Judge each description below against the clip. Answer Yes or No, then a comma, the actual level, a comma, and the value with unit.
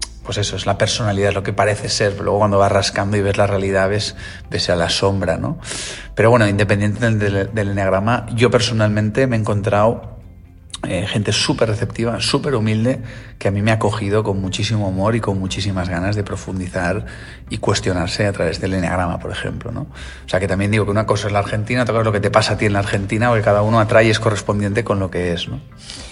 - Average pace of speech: No, fast, 230 wpm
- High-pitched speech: No, low, 105 Hz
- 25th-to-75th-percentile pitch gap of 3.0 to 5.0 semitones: No, narrow, 2.6 semitones